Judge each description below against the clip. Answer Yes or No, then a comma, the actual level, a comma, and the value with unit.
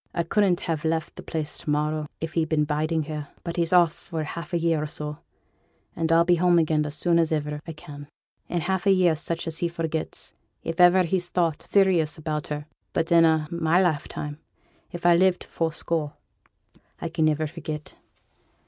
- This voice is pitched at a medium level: Yes, medium, 165 Hz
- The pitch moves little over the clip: Yes, narrow, 2.0 semitones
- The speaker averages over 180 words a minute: Yes, average, 200 wpm